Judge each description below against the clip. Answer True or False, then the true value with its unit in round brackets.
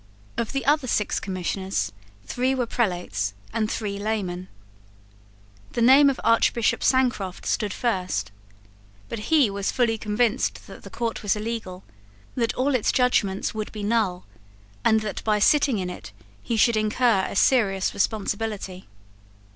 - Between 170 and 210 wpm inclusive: False (145 wpm)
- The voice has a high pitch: True (215 Hz)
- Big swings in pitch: False (3.7 semitones)